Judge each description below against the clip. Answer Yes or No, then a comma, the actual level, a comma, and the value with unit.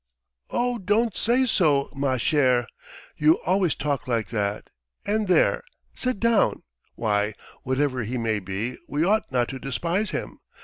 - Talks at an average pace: Yes, average, 145 wpm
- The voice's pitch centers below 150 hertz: Yes, medium, 140 Hz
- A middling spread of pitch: No, wide, 9.0 semitones